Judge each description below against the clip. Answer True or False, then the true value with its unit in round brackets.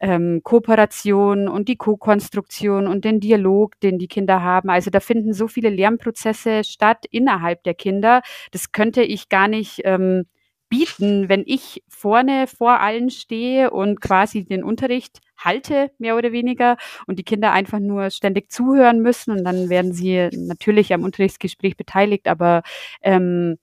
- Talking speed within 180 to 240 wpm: False (155 wpm)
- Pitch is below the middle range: False (210 Hz)